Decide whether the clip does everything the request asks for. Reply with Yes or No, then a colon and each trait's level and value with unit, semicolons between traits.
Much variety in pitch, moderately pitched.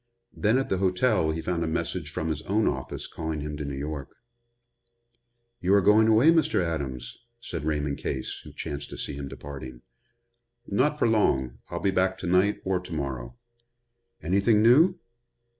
No: wide, 6.4 semitones; very low, 85 Hz